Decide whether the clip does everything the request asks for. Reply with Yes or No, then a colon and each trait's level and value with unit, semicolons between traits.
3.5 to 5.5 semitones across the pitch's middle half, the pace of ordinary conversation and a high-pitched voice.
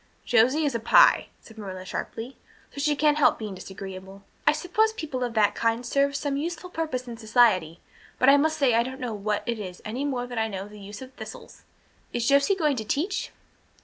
No: average, 5.2 semitones; fast, 210 wpm; high, 245 Hz